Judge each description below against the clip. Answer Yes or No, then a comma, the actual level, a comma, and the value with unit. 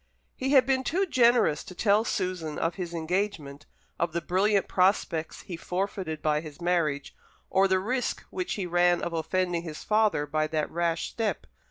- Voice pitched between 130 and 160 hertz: No, medium, 180 Hz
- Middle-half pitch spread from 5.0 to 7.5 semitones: No, average, 4.2 semitones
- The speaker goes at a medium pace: Yes, average, 175 wpm